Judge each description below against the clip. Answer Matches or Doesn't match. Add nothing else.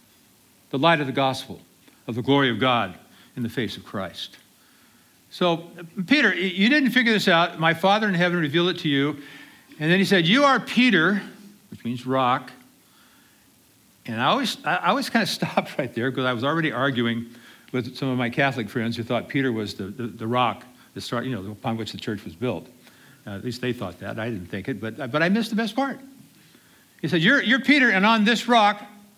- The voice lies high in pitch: Doesn't match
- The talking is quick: Matches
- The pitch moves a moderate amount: Doesn't match